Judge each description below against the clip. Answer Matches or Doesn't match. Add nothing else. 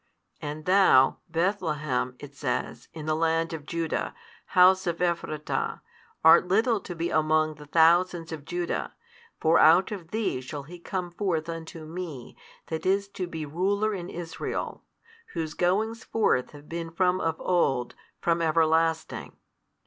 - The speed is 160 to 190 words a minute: Doesn't match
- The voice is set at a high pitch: Doesn't match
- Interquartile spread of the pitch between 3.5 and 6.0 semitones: Doesn't match